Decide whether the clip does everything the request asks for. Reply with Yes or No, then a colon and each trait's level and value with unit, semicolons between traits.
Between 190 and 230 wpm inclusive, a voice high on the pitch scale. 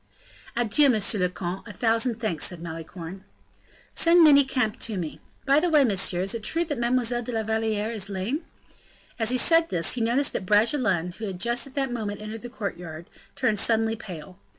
Yes: average, 195 wpm; high, 225 Hz